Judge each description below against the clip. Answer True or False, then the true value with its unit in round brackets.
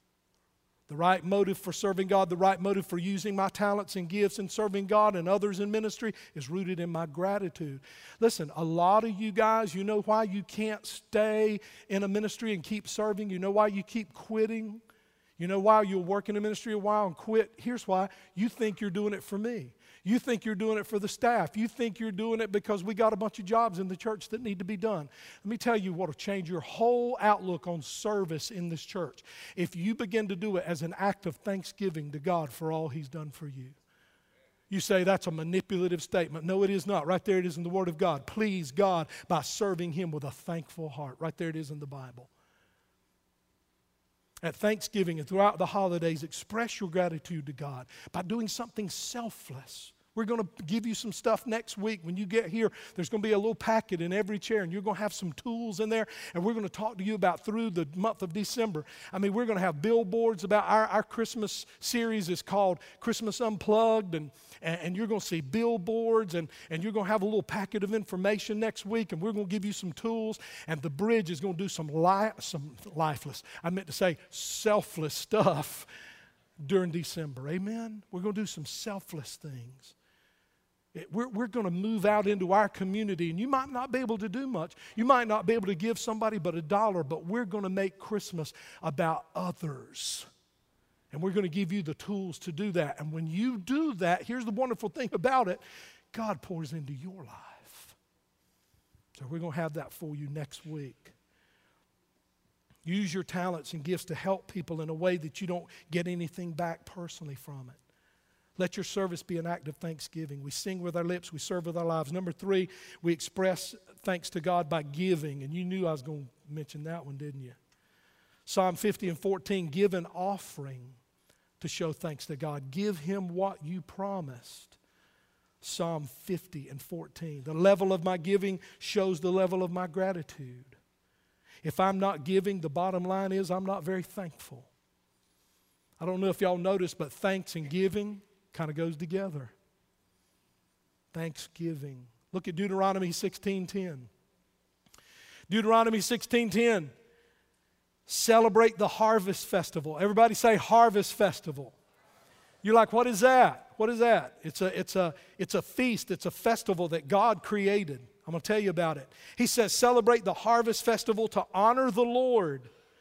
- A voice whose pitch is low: False (190 Hz)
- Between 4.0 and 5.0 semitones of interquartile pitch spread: True (4.3 semitones)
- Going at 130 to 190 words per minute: False (200 wpm)